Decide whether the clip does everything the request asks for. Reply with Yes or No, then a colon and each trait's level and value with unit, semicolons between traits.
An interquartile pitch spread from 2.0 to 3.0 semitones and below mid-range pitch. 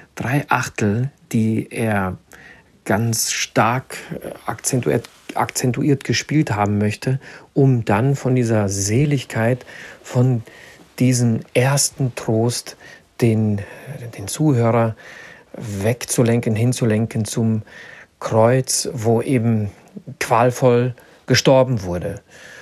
Yes: average, 2.7 semitones; low, 120 Hz